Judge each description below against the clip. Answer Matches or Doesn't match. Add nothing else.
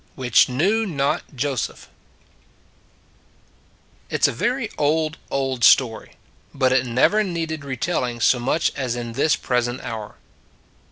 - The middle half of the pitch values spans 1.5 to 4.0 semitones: Doesn't match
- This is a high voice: Doesn't match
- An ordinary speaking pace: Doesn't match